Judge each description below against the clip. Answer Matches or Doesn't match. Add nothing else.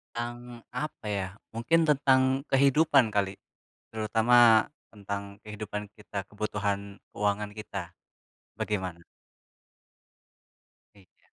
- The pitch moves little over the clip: Doesn't match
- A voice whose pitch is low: Matches